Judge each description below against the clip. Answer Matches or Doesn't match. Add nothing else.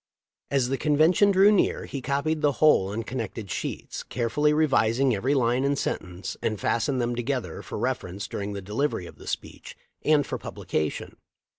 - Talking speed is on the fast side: Doesn't match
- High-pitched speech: Doesn't match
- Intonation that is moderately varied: Matches